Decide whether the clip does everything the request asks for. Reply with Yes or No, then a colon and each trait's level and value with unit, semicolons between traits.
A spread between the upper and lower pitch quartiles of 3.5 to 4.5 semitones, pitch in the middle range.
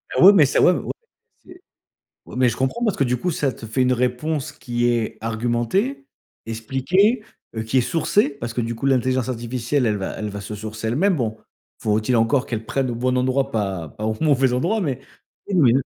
No: average, 3.9 semitones; low, 125 Hz